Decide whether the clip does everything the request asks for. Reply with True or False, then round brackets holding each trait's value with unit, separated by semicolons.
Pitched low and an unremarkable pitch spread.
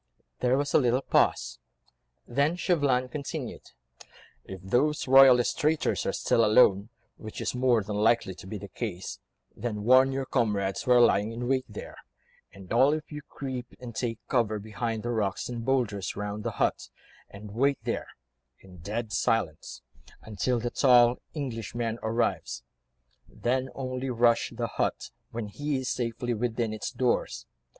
True (120 Hz; 3.3 semitones)